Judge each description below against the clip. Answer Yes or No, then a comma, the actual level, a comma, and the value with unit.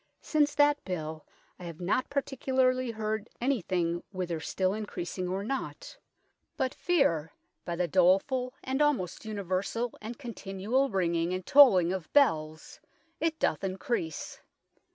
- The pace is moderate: No, slow, 130 wpm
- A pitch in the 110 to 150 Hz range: No, high, 200 Hz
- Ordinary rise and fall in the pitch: No, wide, 6.7 semitones